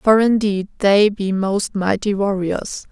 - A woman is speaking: Yes, female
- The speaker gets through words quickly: No, average, 145 wpm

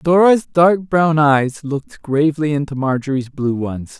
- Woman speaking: No, male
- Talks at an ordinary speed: Yes, average, 150 wpm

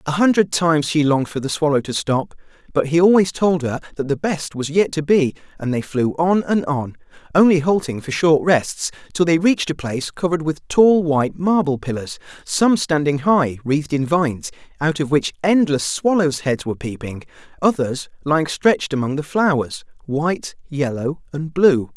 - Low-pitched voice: No, medium, 155 Hz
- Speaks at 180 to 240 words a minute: Yes, average, 185 wpm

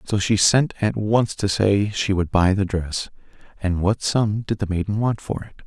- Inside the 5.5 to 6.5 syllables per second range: No, 4.5 syllables/s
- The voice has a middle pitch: No, low, 100 Hz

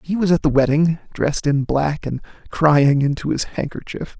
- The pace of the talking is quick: No, average, 185 wpm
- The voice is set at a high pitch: No, medium, 150 Hz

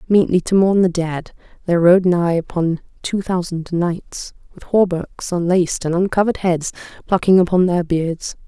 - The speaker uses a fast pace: No, average, 155 wpm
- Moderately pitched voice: Yes, medium, 175 Hz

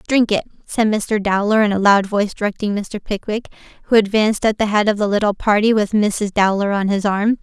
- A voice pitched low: No, high, 210 Hz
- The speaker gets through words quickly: Yes, fast, 220 wpm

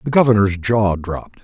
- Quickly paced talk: No, average, 165 wpm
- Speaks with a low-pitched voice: Yes, low, 105 Hz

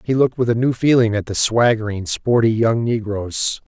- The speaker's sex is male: Yes, male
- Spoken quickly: No, average, 190 wpm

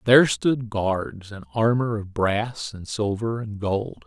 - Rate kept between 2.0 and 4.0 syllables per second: Yes, 3.7 syllables/s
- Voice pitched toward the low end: Yes, low, 110 Hz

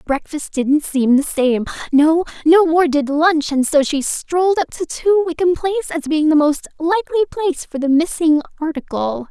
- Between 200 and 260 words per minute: No, average, 180 wpm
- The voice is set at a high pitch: Yes, very high, 315 Hz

